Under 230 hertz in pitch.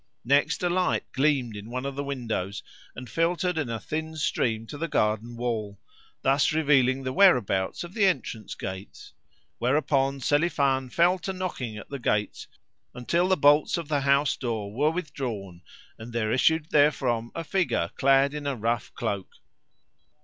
Yes: low, 135 Hz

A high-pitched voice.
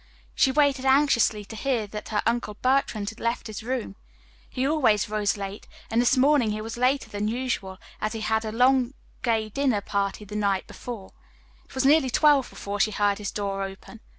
Yes: high, 225 Hz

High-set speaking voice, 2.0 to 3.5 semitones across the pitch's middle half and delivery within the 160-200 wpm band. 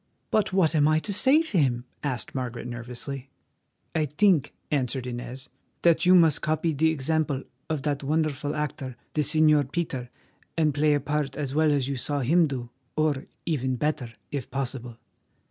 No: medium, 145 Hz; average, 3.1 semitones; average, 170 wpm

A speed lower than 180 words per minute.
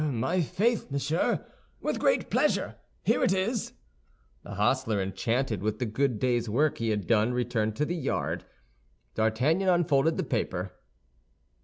Yes: average, 145 wpm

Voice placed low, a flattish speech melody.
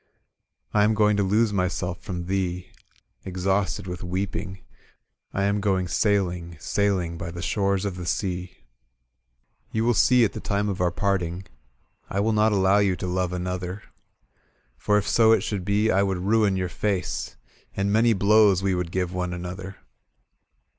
Yes: very low, 95 Hz; narrow, 2.3 semitones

